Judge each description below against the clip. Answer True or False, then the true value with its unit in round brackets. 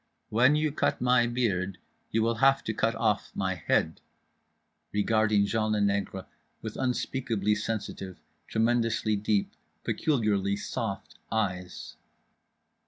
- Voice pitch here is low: True (110 Hz)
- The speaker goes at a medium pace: False (115 wpm)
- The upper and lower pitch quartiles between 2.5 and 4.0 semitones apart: True (2.8 semitones)